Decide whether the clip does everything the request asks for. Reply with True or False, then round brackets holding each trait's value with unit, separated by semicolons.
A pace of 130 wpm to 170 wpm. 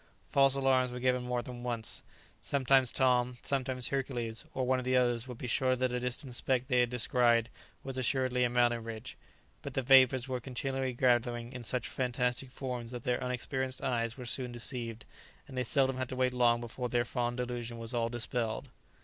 False (195 wpm)